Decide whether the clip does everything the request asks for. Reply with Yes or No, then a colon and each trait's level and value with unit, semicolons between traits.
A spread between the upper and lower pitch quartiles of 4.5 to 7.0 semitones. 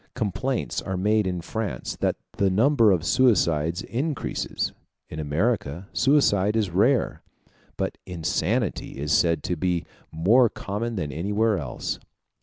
Yes: average, 5.1 semitones